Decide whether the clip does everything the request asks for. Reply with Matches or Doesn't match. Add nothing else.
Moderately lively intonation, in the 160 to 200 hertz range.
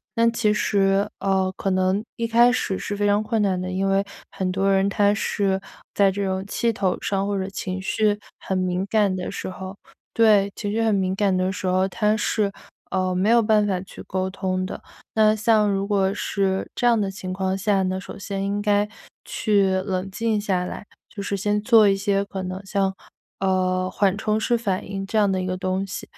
Doesn't match